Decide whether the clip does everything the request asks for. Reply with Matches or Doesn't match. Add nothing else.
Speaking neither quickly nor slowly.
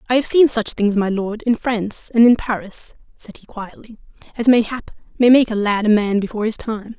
Doesn't match